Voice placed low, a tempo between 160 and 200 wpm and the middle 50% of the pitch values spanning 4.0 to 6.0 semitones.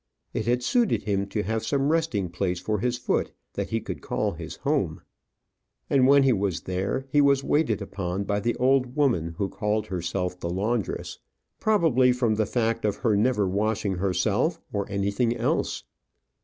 Yes: low, 110 Hz; average, 175 wpm; average, 4.5 semitones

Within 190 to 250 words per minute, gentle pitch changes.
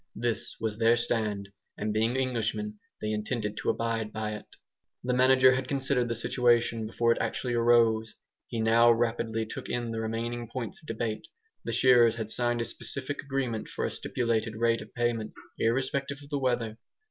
No: average, 175 wpm; narrow, 1.7 semitones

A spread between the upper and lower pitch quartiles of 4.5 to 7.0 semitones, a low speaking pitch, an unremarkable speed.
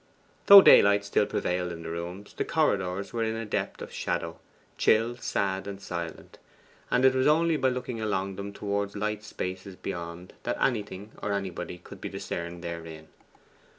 No: average, 3.8 semitones; low, 100 Hz; average, 170 wpm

